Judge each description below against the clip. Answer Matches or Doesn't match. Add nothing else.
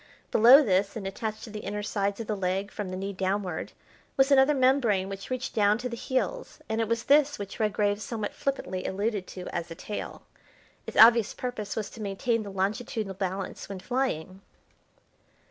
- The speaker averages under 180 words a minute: Doesn't match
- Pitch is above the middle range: Matches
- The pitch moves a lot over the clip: Doesn't match